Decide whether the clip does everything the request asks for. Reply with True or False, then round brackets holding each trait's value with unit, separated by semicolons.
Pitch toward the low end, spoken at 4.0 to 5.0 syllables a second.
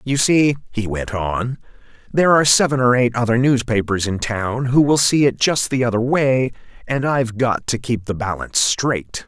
True (125 Hz; 4.9 syllables/s)